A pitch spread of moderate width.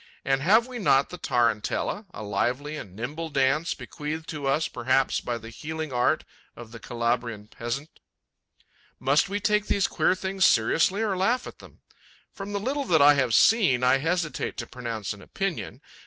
No: wide, 7.5 semitones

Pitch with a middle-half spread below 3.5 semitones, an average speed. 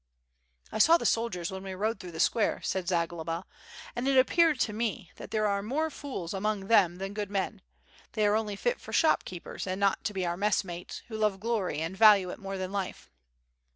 No: average, 3.0 semitones; fast, 215 wpm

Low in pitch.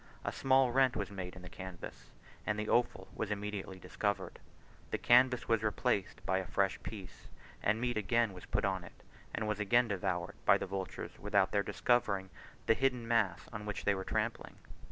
Yes: low, 105 Hz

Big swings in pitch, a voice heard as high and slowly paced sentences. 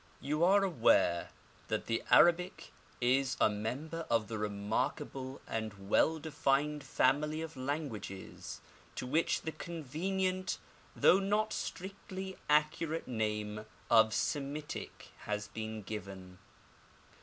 No: wide, 6.9 semitones; medium, 140 Hz; slow, 110 wpm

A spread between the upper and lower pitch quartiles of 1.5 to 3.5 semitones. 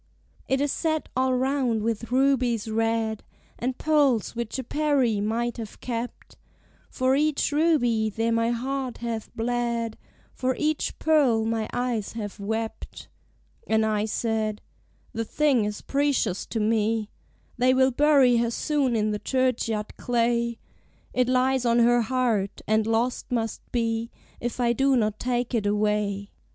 Yes: average, 2.7 semitones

